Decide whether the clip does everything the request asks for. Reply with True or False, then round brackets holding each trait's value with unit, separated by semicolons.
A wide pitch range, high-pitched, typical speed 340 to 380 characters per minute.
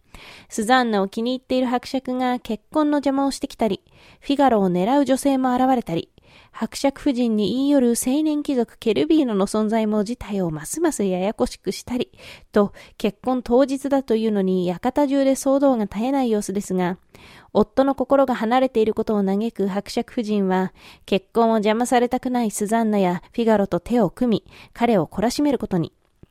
False (4.2 semitones; 235 Hz; 360 characters per minute)